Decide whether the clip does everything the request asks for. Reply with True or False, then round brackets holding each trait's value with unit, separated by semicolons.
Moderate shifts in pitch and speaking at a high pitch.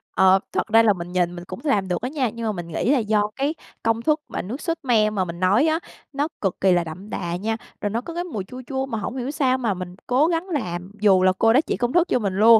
False (6.2 semitones; 225 Hz)